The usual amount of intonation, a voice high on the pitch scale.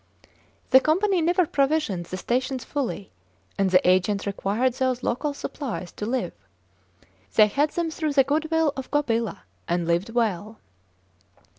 No: wide, 6.7 semitones; very high, 255 Hz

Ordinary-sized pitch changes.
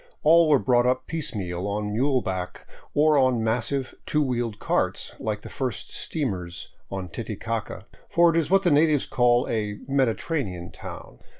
No: wide, 6.0 semitones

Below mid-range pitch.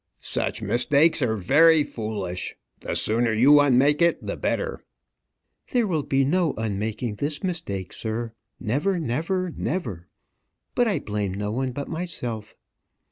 Yes: low, 130 Hz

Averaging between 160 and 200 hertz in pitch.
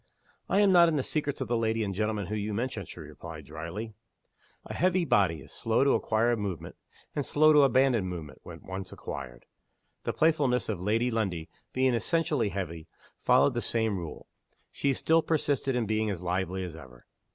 No: low, 110 Hz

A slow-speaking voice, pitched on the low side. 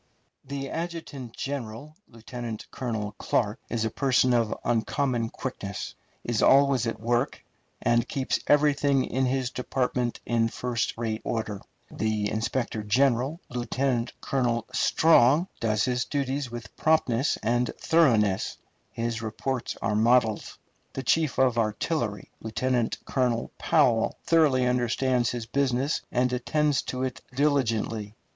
Yes: slow, 125 wpm; low, 125 Hz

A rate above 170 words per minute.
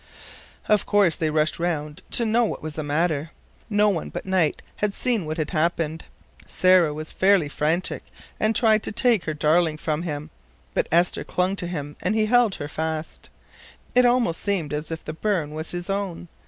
Yes: average, 195 wpm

